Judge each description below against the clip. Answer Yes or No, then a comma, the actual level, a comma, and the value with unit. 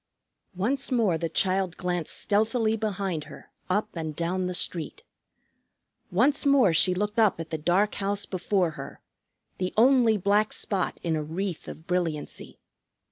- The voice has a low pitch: No, medium, 185 Hz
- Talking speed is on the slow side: No, average, 150 wpm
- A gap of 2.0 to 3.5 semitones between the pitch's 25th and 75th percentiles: No, average, 3.9 semitones